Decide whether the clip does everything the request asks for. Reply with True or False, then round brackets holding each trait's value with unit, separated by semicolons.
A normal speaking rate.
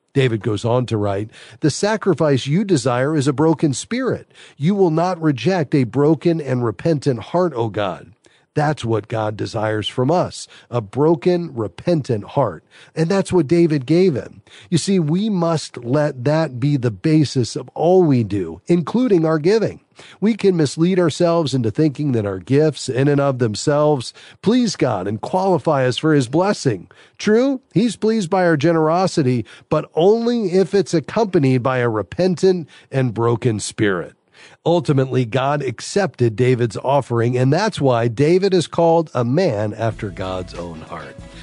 True (160 wpm)